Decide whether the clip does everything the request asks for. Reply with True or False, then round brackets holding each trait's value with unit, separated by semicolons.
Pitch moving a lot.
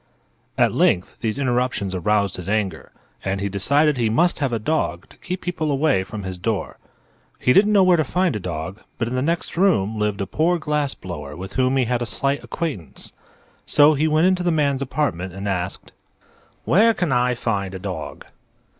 True (7.9 semitones)